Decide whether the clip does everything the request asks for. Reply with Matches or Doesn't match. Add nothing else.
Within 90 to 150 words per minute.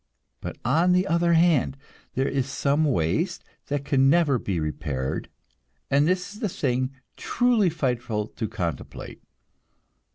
Matches